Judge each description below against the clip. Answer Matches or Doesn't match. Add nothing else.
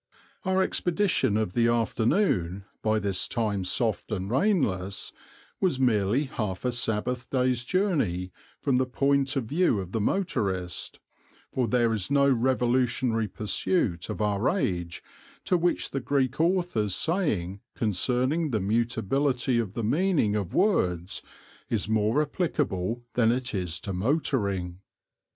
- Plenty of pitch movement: Matches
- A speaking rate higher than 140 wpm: Doesn't match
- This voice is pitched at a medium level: Doesn't match